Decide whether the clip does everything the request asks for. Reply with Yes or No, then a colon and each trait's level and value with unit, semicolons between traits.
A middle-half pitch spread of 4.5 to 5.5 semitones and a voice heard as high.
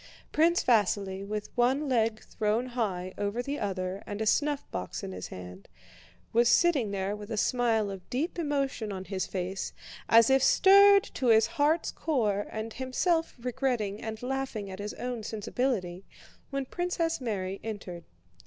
Yes: average, 5.1 semitones; high, 225 Hz